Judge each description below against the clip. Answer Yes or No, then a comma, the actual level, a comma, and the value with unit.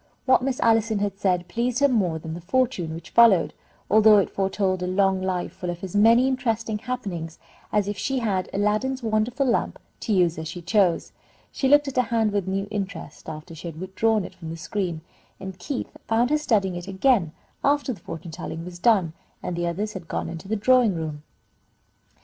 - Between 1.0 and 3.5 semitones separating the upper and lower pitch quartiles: No, average, 4.6 semitones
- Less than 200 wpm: No, fast, 205 wpm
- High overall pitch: Yes, high, 200 Hz